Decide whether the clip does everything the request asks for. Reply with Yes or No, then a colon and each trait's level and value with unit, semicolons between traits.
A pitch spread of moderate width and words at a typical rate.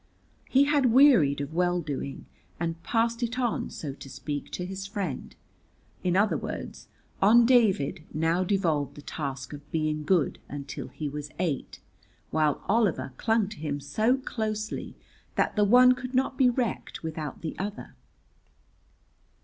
No: wide, 7.4 semitones; average, 150 wpm